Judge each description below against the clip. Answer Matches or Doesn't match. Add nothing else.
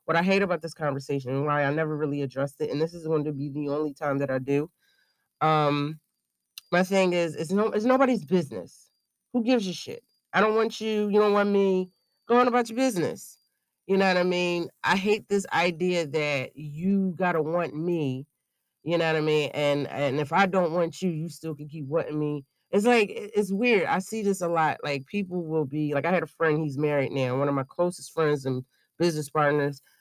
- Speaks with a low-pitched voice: Doesn't match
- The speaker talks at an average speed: Doesn't match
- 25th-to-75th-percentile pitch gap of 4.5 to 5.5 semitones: Matches